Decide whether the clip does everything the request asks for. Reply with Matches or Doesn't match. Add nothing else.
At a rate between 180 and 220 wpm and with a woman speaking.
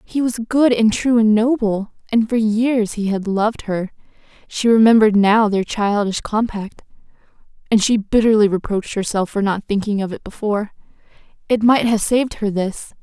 Doesn't match